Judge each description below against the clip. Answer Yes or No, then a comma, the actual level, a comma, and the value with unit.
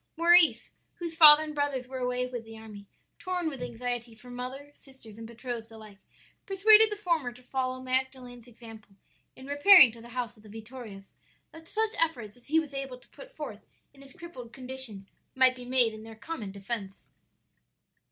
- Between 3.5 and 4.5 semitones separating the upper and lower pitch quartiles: Yes, average, 4.1 semitones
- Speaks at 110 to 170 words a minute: No, average, 180 wpm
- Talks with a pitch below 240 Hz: No, very high, 250 Hz